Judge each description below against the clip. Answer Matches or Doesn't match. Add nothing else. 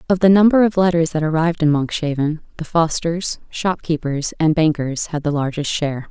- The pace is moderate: Matches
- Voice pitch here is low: Doesn't match